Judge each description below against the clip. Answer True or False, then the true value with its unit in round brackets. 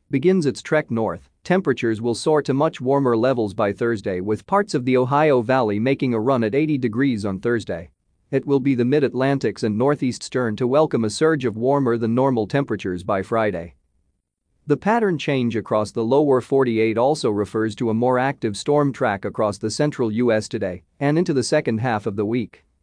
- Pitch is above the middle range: False (120 Hz)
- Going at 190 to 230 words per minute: True (195 wpm)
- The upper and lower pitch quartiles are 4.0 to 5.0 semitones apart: True (4.3 semitones)